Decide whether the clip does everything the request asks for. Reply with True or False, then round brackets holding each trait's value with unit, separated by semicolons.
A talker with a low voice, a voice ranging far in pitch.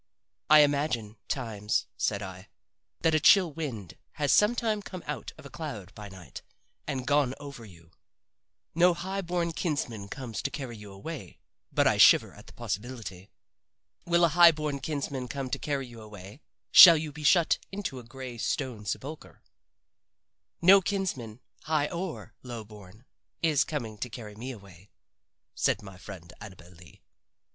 True (130 Hz; 6.9 semitones)